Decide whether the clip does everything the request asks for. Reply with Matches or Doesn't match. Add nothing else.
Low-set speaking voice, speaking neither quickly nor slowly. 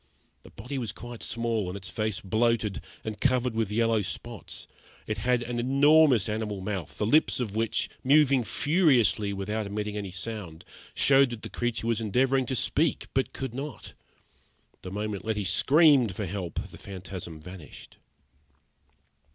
Matches